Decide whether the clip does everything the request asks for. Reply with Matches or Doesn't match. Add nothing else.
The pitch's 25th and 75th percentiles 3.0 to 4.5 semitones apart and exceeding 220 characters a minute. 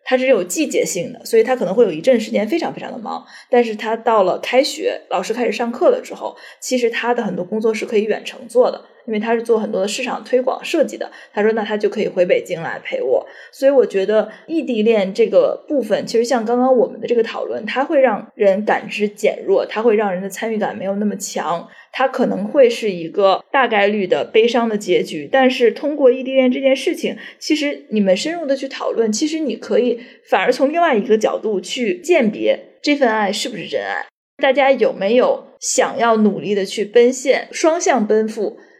Doesn't match